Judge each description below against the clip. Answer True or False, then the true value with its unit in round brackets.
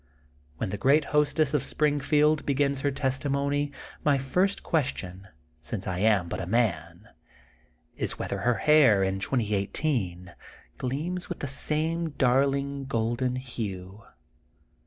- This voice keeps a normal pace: False (130 wpm)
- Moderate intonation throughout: False (6.0 semitones)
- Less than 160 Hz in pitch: True (135 Hz)